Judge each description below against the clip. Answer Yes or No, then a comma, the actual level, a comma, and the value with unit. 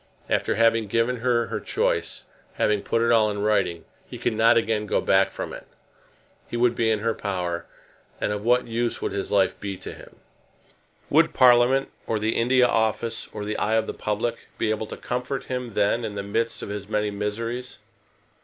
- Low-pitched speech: Yes, low, 110 Hz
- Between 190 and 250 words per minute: Yes, average, 200 wpm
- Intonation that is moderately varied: No, narrow, 2.3 semitones